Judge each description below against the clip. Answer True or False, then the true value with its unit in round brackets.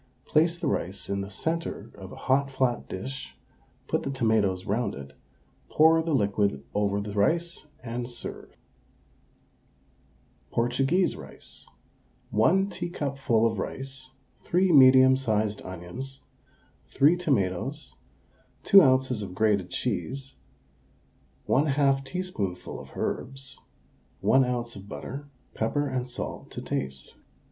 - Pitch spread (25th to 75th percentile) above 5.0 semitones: True (5.4 semitones)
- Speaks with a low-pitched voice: True (130 Hz)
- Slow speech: True (120 wpm)